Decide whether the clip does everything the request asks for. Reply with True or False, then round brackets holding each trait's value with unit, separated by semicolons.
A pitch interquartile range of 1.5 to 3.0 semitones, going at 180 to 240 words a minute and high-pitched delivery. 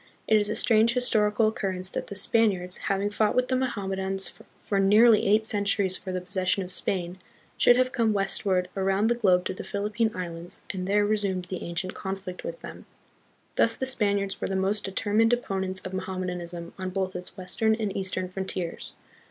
True (2.5 semitones; 185 wpm; 195 Hz)